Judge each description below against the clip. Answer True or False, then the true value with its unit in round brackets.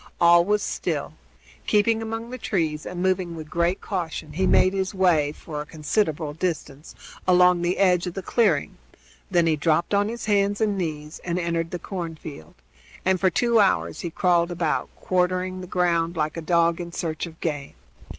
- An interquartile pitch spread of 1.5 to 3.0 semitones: True (2.6 semitones)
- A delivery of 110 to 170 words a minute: False (180 wpm)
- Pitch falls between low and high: True (175 Hz)